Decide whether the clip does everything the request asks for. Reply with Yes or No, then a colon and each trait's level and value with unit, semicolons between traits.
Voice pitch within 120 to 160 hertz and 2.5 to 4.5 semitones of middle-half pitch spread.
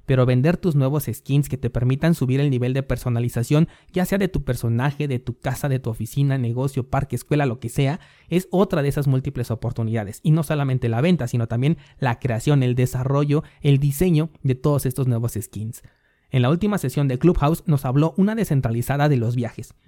Yes: low, 135 Hz; average, 3.4 semitones